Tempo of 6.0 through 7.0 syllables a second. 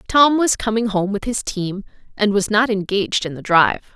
No: 5.2 syllables/s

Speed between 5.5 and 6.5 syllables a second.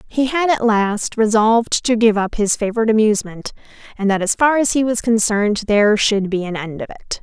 Yes: 5.7 syllables/s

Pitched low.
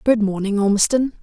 No: high, 215 Hz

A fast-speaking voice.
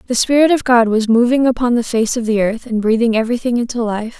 Yes: fast, 245 wpm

